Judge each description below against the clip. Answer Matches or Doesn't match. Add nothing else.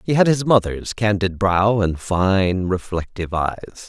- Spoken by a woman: Doesn't match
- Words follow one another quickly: Doesn't match